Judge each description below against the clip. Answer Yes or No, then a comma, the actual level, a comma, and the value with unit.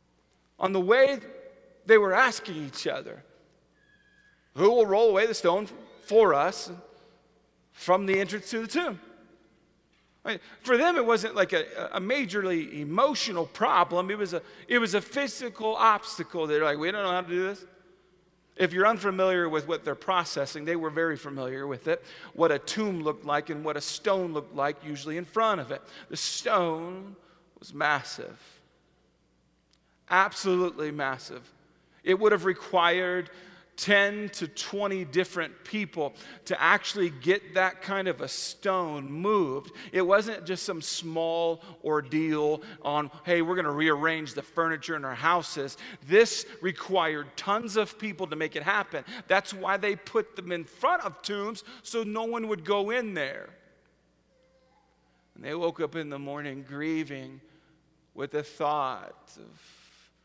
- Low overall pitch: No, medium, 180 Hz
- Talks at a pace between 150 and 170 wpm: Yes, average, 155 wpm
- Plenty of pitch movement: No, average, 4.6 semitones